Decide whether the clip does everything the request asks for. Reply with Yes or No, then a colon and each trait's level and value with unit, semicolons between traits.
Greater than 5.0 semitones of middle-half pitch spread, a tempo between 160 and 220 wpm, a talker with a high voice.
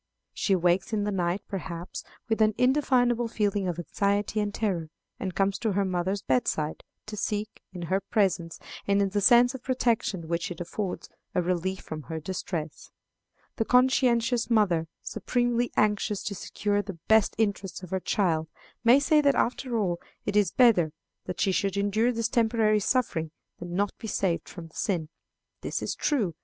No: average, 4.1 semitones; average, 175 wpm; high, 200 Hz